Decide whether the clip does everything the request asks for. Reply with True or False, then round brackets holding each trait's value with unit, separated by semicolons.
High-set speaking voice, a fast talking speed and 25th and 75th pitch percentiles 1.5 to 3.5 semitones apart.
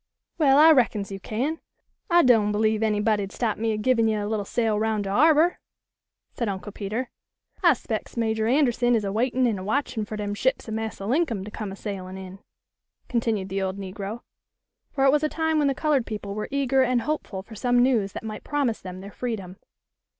False (220 Hz; 210 wpm; 4.0 semitones)